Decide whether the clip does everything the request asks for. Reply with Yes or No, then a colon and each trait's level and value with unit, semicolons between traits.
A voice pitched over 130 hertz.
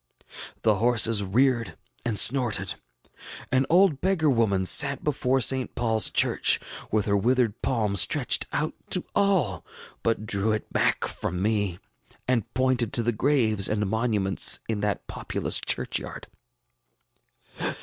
No: low, 115 Hz